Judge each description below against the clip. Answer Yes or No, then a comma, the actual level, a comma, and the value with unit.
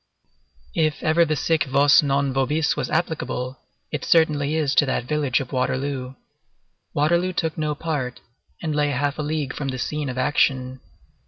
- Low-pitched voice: No, medium, 145 Hz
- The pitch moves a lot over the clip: No, average, 2.8 semitones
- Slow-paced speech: No, average, 165 wpm